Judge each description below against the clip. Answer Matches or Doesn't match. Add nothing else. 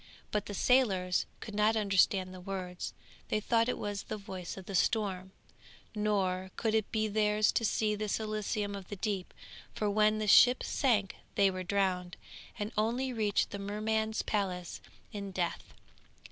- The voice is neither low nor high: Doesn't match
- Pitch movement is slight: Matches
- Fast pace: Doesn't match